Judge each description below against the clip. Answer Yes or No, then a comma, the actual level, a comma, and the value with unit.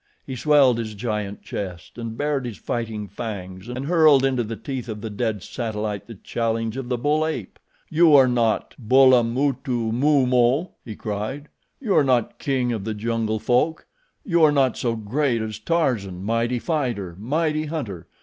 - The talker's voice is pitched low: Yes, low, 120 Hz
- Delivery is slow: No, average, 165 wpm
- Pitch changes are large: No, average, 4.1 semitones